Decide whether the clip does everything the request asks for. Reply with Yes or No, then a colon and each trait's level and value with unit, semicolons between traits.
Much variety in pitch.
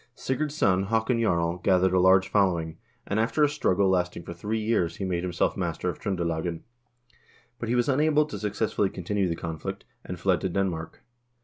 No: average, 4.3 semitones